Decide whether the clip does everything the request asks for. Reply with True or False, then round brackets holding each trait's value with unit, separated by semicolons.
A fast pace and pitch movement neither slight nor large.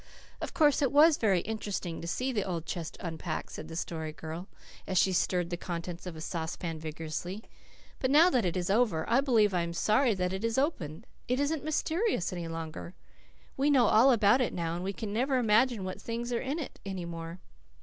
False (210 wpm; 6.6 semitones)